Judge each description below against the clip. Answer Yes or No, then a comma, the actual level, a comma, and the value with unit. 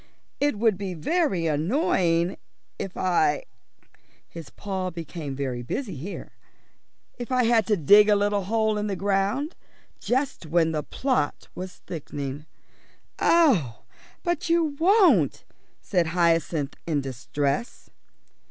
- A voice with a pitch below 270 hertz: Yes, high, 190 Hz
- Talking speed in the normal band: No, slow, 125 wpm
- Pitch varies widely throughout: Yes, wide, 6.8 semitones